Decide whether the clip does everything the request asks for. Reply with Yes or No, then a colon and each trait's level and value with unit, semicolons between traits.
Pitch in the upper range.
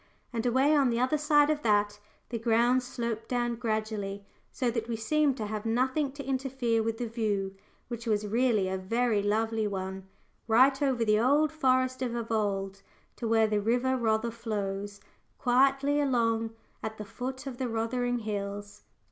Yes: high, 230 Hz